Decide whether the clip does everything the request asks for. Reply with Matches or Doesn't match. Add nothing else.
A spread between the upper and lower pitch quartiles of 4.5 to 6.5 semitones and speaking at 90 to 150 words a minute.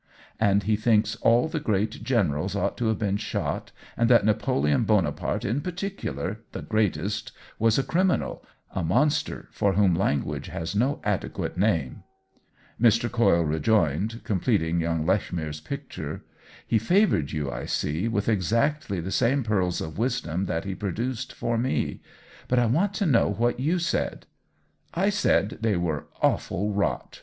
Doesn't match